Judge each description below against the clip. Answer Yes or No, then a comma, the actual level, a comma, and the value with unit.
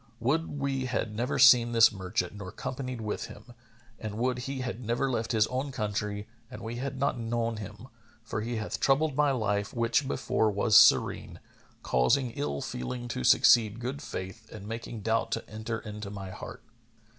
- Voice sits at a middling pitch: No, low, 115 Hz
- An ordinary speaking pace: Yes, average, 180 wpm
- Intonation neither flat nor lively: Yes, average, 3.4 semitones